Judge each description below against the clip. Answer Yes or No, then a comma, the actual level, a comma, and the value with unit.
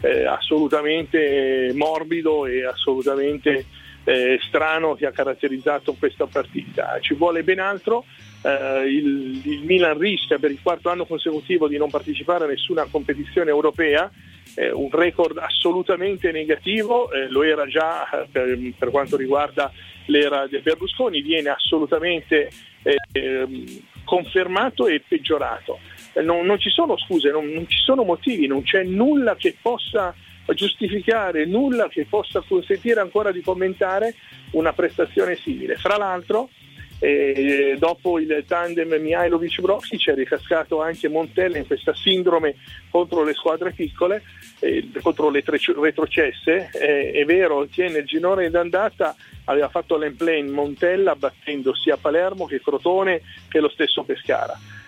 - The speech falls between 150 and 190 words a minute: No, average, 135 wpm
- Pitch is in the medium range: Yes, medium, 165 Hz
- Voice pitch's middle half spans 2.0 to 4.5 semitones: No, wide, 5.6 semitones